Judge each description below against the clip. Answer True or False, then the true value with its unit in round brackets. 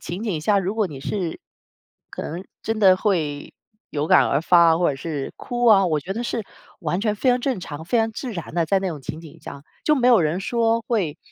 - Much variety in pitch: True (5.7 semitones)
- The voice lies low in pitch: False (185 Hz)